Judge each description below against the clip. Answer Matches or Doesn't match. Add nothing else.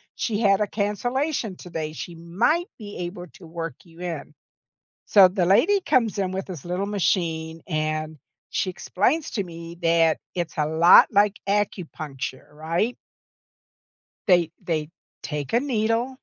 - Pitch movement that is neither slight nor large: Matches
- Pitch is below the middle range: Doesn't match